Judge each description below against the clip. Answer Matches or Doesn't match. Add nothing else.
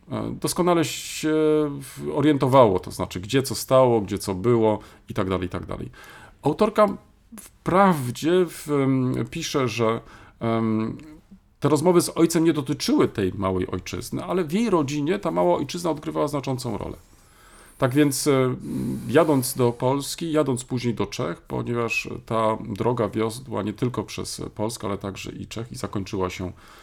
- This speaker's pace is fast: Doesn't match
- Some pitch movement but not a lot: Doesn't match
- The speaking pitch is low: Matches